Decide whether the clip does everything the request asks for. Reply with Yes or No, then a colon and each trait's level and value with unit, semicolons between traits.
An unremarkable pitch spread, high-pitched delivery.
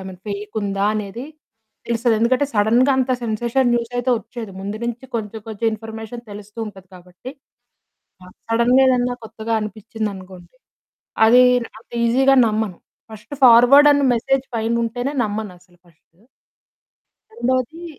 Yes: average, 3.0 semitones; high, 225 Hz